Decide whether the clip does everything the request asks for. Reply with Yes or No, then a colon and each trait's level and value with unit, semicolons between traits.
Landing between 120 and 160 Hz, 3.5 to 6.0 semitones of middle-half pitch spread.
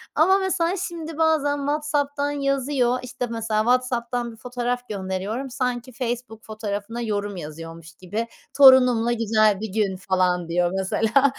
No: high, 240 Hz; average, 4.8 semitones